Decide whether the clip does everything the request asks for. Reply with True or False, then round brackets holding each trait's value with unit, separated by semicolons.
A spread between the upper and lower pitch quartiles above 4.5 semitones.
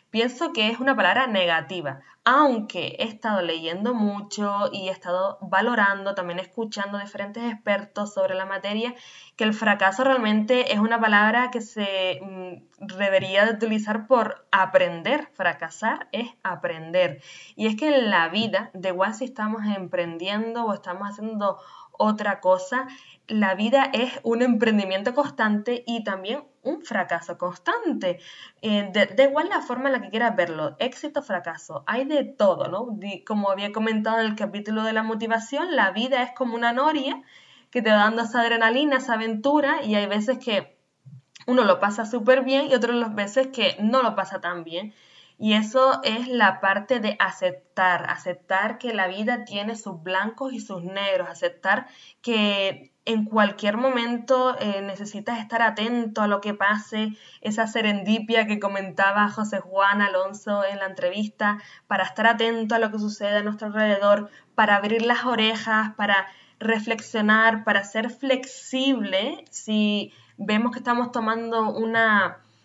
False (3.5 semitones)